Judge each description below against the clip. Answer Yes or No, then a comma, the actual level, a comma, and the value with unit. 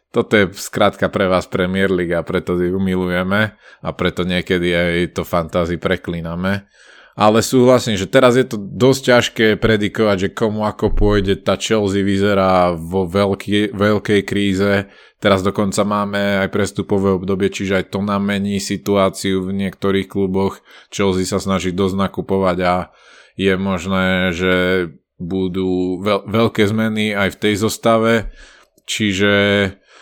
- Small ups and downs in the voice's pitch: Yes, narrow, 1.8 semitones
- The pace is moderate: Yes, average, 145 wpm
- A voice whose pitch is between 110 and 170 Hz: No, low, 100 Hz